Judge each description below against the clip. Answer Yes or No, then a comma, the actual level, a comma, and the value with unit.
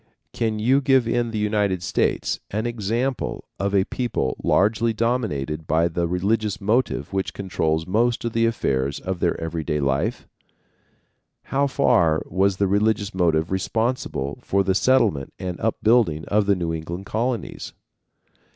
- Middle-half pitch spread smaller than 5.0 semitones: No, average, 5.3 semitones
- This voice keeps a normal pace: Yes, average, 150 wpm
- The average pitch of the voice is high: No, low, 100 Hz